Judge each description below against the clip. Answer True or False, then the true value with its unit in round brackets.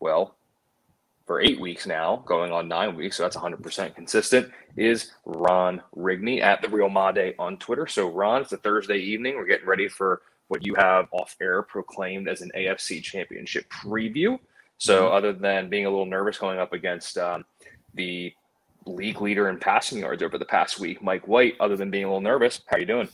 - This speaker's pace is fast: False (195 wpm)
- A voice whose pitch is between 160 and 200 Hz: False (95 Hz)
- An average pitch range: False (1.9 semitones)